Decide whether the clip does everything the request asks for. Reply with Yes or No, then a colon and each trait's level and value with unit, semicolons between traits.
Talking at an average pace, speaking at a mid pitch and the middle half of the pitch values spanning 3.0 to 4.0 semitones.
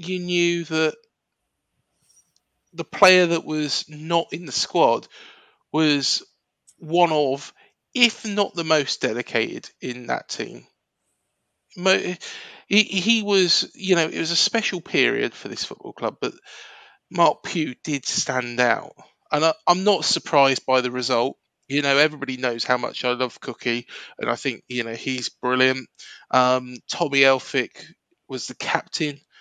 No: average, 145 wpm; medium, 150 Hz; wide, 5.5 semitones